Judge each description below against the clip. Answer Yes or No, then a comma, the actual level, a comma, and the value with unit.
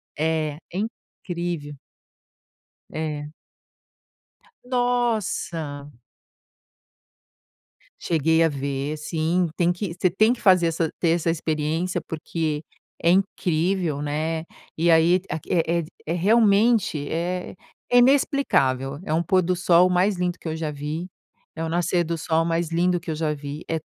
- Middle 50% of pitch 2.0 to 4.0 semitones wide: Yes, narrow, 2.6 semitones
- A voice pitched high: No, medium, 165 Hz